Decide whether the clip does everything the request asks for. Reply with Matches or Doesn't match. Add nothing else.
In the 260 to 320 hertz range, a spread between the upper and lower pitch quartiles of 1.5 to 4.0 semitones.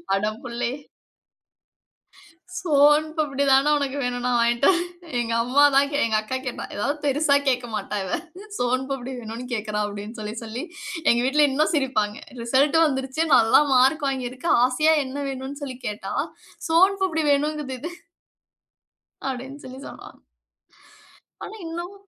Matches